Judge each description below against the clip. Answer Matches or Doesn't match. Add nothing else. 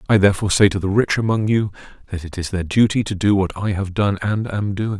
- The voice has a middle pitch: Doesn't match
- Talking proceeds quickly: Matches